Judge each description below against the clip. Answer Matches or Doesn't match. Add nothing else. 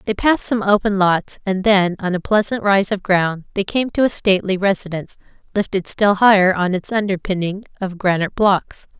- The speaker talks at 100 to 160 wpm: Doesn't match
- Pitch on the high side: Matches